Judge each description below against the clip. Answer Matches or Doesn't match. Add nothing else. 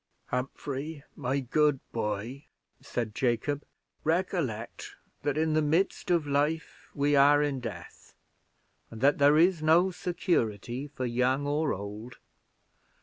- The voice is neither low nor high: Matches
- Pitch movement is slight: Doesn't match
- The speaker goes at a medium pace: Doesn't match